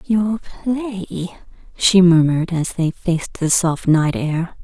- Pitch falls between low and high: Yes, medium, 180 Hz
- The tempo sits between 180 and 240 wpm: No, average, 140 wpm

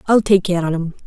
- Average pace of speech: No, fast, 280 wpm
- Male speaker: No, female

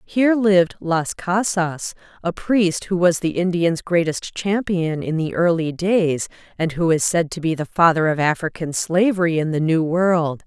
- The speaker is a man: No, female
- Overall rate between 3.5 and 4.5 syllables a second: Yes, 4.4 syllables/s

